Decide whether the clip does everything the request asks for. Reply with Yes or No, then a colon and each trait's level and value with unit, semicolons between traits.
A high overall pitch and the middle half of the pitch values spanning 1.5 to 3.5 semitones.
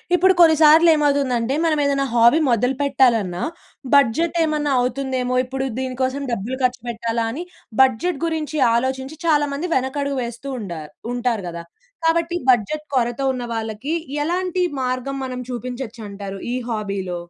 No: very high, 260 Hz; average, 4.0 semitones